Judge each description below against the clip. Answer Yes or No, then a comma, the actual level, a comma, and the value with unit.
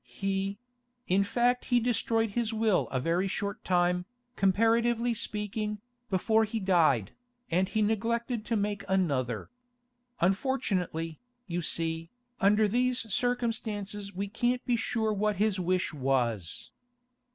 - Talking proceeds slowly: Yes, slow, 120 wpm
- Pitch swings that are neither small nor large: Yes, average, 4.1 semitones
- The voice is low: No, high, 205 Hz